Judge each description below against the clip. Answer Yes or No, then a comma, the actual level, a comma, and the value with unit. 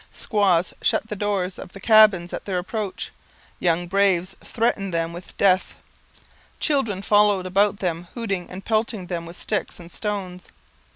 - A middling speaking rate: Yes, average, 155 wpm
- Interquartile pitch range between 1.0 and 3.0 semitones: Yes, average, 2.7 semitones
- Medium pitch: No, high, 195 Hz